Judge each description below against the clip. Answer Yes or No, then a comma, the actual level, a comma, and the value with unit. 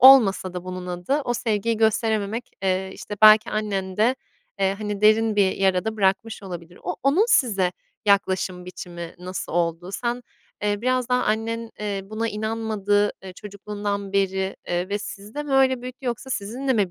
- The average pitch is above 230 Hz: No, high, 205 Hz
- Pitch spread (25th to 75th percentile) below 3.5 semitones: Yes, average, 3.1 semitones